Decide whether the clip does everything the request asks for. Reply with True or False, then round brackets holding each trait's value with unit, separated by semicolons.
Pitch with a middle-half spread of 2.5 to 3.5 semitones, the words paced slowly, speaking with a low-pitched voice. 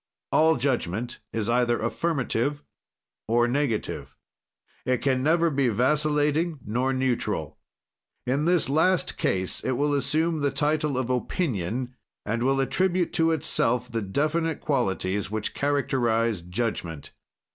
False (4.4 semitones; 125 wpm; 130 Hz)